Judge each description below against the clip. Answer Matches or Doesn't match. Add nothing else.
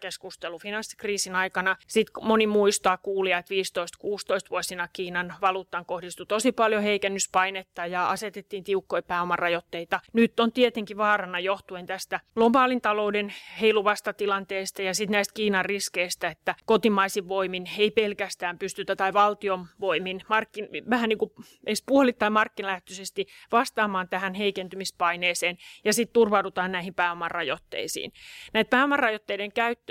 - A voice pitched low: Doesn't match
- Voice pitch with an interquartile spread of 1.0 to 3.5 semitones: Matches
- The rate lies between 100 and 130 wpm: Matches